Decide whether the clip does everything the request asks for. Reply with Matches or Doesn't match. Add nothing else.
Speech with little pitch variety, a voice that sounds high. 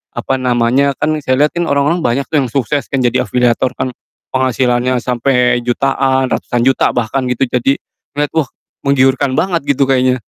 Doesn't match